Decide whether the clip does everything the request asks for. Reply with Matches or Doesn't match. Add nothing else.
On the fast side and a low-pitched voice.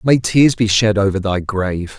Matches